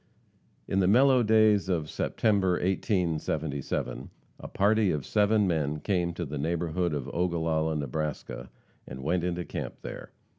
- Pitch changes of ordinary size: Yes, average, 4.3 semitones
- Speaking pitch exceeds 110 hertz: No, very low, 85 Hz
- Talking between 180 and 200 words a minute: No, average, 140 wpm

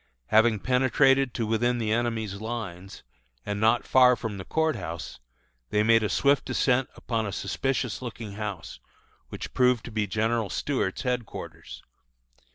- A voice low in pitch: Yes, low, 115 Hz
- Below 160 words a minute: Yes, average, 150 wpm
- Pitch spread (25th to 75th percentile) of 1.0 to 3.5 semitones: Yes, average, 3.1 semitones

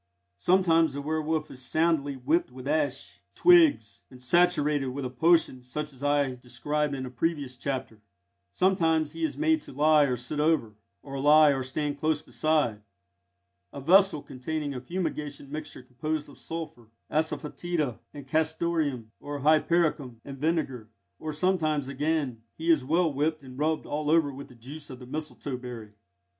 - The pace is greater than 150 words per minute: Yes, average, 160 wpm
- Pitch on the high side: No, medium, 150 Hz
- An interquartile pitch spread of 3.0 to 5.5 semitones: Yes, average, 3.4 semitones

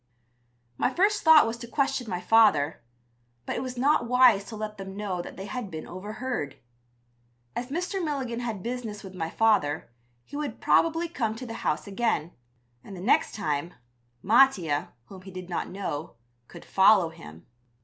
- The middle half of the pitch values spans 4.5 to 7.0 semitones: Yes, wide, 5.4 semitones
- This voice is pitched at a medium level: No, high, 215 Hz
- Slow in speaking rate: No, average, 170 wpm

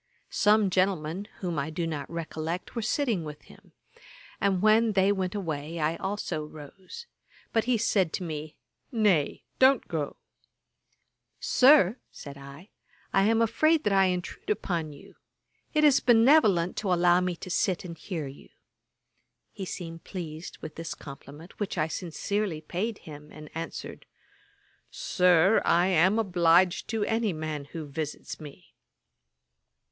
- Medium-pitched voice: Yes, medium, 180 Hz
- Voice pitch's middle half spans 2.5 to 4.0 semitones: No, average, 4.8 semitones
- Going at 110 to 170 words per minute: Yes, average, 145 wpm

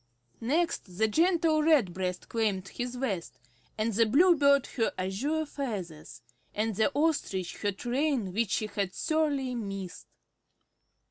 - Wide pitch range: Yes, wide, 7.0 semitones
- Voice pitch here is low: No, high, 230 Hz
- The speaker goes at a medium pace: No, slow, 125 wpm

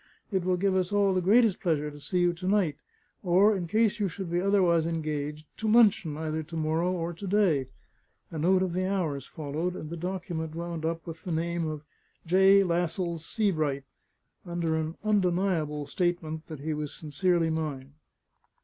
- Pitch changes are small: No, average, 3.0 semitones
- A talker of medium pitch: Yes, medium, 170 Hz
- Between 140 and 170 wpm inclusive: No, average, 180 wpm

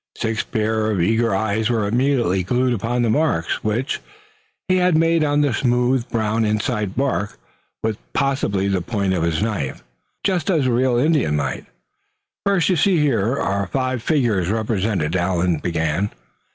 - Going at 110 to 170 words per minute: Yes, average, 160 wpm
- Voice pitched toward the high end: No, low, 110 Hz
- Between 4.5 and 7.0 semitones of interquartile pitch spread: Yes, average, 5.1 semitones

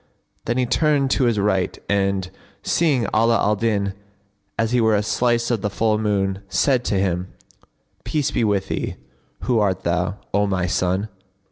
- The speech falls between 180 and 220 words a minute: No, average, 170 wpm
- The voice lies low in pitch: Yes, low, 105 Hz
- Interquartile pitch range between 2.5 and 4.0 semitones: Yes, average, 3.4 semitones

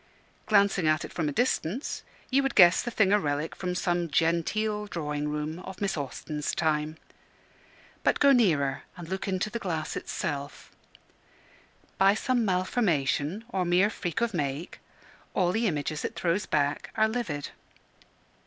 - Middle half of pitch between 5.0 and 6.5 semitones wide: Yes, wide, 5.5 semitones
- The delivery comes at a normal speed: Yes, average, 155 wpm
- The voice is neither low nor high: Yes, medium, 175 Hz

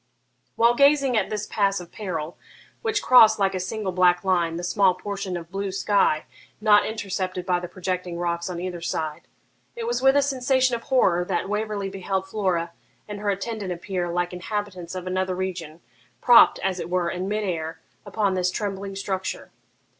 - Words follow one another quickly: No, average, 180 wpm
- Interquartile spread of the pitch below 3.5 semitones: Yes, average, 2.9 semitones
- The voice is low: No, high, 190 Hz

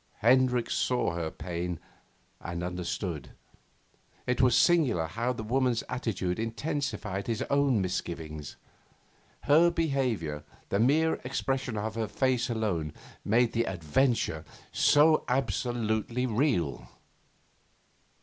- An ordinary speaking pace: No, slow, 105 wpm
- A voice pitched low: Yes, low, 115 Hz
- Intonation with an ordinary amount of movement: No, wide, 6.5 semitones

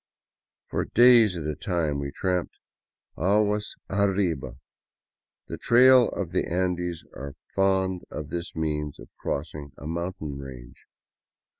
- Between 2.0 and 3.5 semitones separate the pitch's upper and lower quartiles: No, average, 4.7 semitones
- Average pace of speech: No, slow, 130 wpm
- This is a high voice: No, very low, 85 Hz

